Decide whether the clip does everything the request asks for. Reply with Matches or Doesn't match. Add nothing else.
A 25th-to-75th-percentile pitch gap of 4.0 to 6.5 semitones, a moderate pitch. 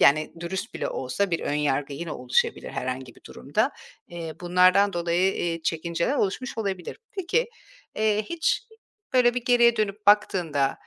Matches